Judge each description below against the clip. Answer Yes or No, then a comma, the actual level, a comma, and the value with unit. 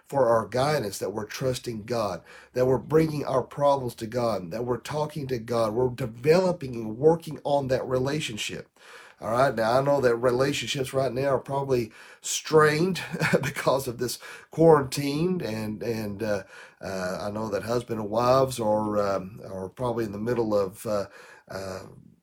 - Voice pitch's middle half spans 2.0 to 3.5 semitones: No, average, 4.2 semitones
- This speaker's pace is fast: No, average, 165 wpm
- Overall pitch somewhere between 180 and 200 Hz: No, low, 125 Hz